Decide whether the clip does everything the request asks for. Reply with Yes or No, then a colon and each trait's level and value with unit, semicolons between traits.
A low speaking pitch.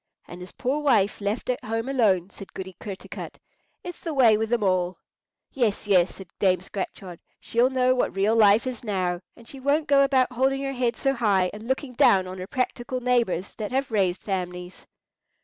No: high, 220 Hz